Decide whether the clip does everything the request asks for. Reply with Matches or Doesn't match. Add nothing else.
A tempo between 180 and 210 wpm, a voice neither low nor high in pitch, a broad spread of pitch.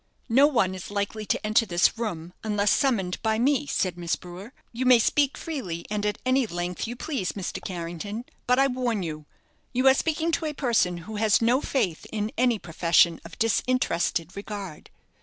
Doesn't match